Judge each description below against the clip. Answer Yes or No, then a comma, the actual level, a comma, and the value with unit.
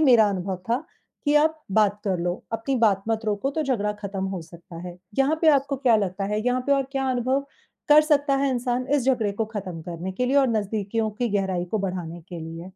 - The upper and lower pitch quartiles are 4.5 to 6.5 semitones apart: Yes, wide, 5.6 semitones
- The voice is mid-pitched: No, high, 220 Hz